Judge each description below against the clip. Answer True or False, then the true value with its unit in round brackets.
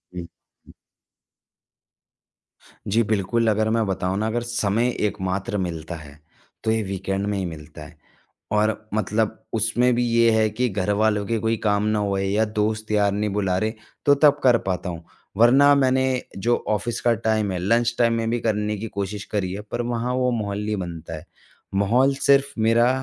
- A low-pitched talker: True (110 Hz)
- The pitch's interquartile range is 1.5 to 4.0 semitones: True (2.9 semitones)